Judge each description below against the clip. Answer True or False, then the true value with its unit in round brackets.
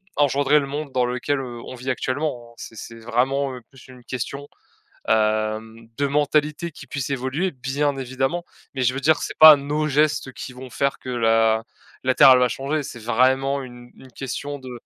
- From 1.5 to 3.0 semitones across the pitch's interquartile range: True (2.7 semitones)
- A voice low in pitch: True (130 Hz)